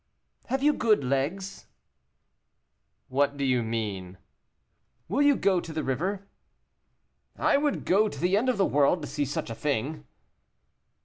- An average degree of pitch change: No, wide, 7.0 semitones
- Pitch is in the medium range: Yes, medium, 155 Hz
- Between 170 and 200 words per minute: No, average, 150 wpm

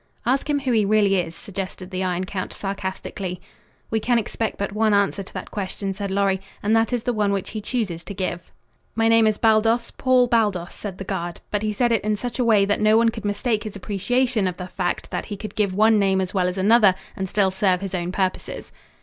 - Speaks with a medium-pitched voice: No, high, 205 Hz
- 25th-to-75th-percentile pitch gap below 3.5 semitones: Yes, average, 2.8 semitones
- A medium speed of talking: No, fast, 235 wpm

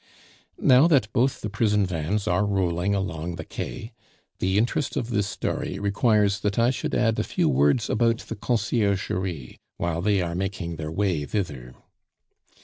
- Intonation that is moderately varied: Yes, average, 4.3 semitones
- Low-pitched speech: Yes, low, 100 Hz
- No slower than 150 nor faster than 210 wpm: Yes, average, 160 wpm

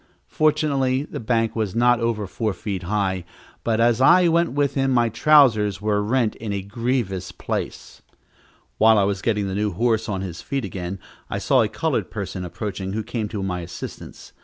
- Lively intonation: No, average, 3.9 semitones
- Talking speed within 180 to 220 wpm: Yes, average, 185 wpm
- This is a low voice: Yes, low, 110 Hz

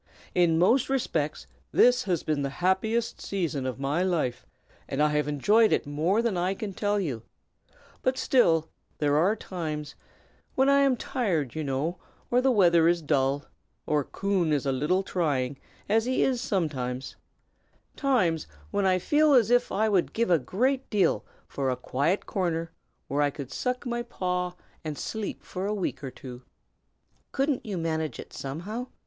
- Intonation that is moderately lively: No, wide, 6.8 semitones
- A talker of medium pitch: Yes, medium, 180 Hz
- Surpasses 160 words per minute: Yes, average, 170 wpm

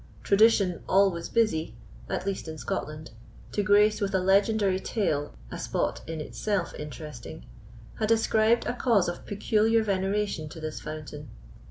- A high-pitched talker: Yes, high, 195 Hz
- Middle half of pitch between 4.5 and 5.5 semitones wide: Yes, average, 5.1 semitones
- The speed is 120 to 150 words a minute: Yes, average, 145 wpm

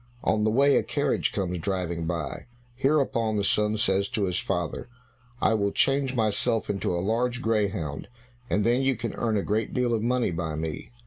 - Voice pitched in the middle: No, low, 105 Hz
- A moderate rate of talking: Yes, average, 190 wpm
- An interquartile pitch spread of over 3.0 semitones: Yes, average, 4.5 semitones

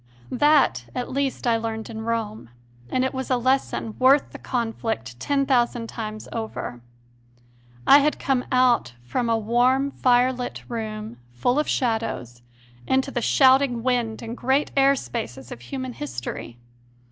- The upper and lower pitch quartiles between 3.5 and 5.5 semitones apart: No, average, 3.0 semitones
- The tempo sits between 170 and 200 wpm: No, average, 145 wpm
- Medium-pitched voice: No, high, 240 Hz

